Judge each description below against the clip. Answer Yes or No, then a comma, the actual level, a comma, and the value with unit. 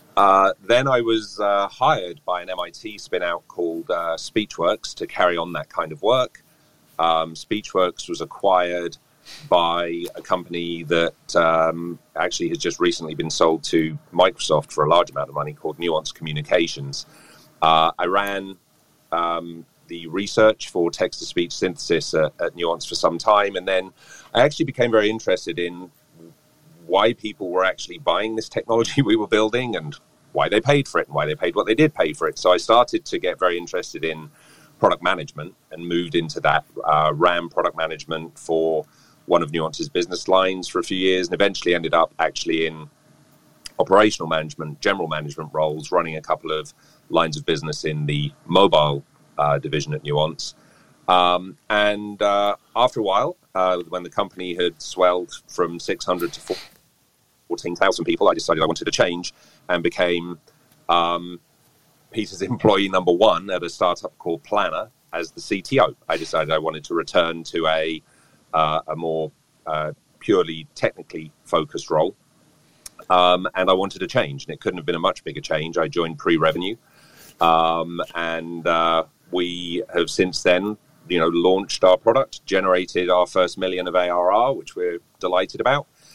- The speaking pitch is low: Yes, very low, 85 Hz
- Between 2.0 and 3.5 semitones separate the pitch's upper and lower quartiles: Yes, average, 2.9 semitones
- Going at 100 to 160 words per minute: No, average, 170 wpm